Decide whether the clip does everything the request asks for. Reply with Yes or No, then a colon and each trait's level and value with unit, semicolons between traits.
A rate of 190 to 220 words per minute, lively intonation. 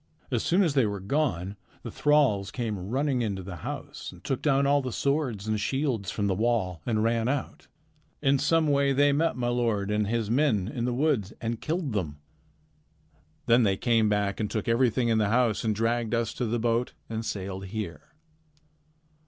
No: average, 195 wpm; average, 4.5 semitones